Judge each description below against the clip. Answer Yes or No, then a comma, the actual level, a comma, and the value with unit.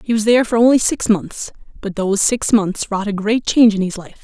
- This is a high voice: Yes, high, 215 Hz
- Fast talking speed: Yes, fast, 255 wpm